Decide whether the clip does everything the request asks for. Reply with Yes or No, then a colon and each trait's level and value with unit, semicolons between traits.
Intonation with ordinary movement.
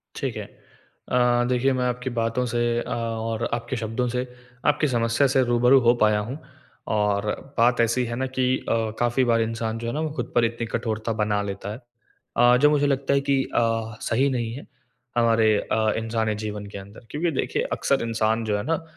No: narrow, 2.2 semitones